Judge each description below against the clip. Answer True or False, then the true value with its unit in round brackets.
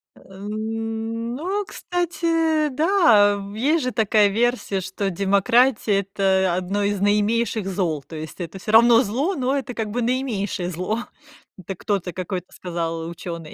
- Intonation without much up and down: False (4.6 semitones)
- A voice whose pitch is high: True (210 Hz)